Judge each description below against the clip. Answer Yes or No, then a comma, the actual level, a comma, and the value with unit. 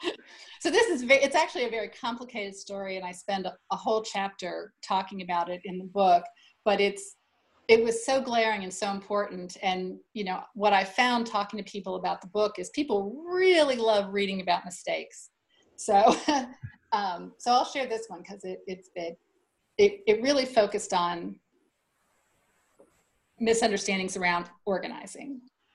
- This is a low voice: No, high, 205 Hz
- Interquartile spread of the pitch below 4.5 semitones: No, average, 4.9 semitones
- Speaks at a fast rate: No, average, 155 wpm